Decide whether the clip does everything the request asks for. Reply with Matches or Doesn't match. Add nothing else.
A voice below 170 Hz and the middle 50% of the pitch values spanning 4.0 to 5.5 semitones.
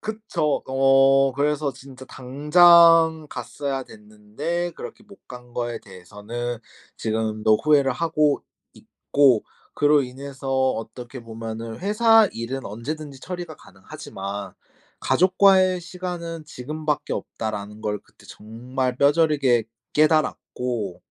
Matches